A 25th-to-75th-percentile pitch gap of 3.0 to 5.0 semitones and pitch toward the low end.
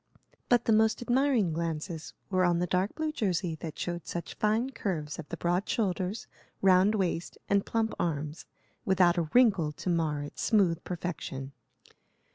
No: average, 4.3 semitones; medium, 180 Hz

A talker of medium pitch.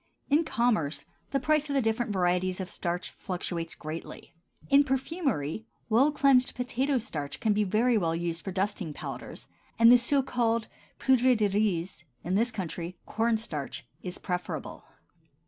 No: high, 220 Hz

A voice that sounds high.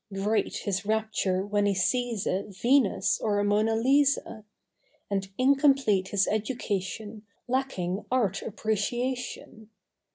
Yes: high, 215 Hz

